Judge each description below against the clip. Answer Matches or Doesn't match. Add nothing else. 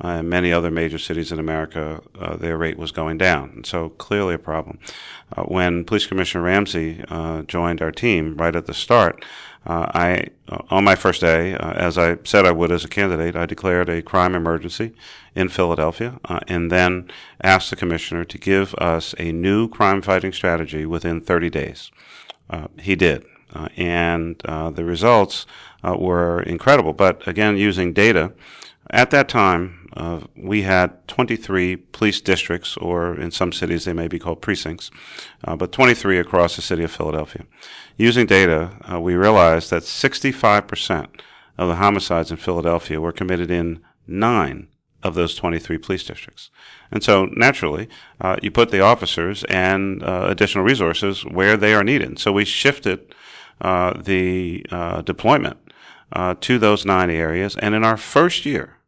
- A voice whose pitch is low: Matches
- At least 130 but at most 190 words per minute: Matches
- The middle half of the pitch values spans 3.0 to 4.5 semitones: Doesn't match